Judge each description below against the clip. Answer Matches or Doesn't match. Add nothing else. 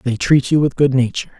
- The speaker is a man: Matches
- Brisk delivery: Matches